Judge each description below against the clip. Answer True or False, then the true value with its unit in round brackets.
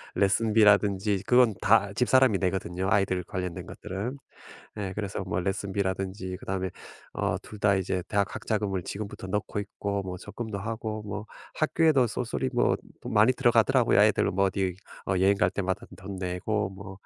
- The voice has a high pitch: False (100 Hz)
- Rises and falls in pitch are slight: True (2.3 semitones)